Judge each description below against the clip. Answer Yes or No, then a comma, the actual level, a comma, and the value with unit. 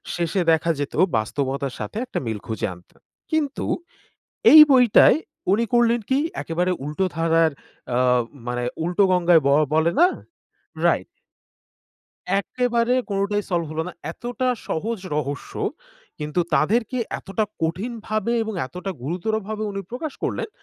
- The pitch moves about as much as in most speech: No, wide, 6.6 semitones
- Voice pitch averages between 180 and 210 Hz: Yes, medium, 185 Hz